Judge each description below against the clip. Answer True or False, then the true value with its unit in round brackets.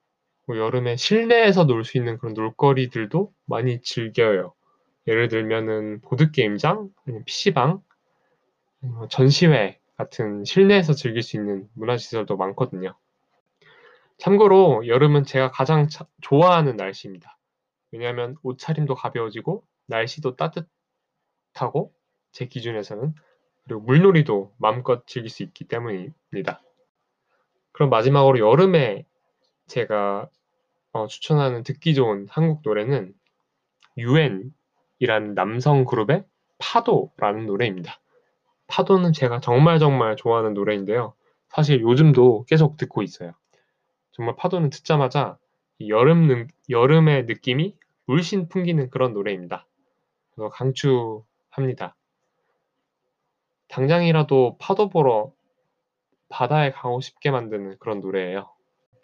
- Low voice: True (130 Hz)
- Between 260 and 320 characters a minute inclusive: True (265 characters per minute)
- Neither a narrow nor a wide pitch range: False (5.7 semitones)